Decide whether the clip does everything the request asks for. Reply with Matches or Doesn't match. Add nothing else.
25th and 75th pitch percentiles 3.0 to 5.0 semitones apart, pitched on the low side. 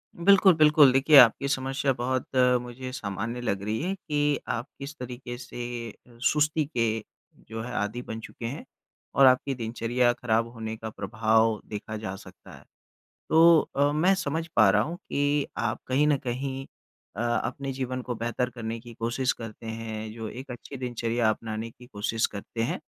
Matches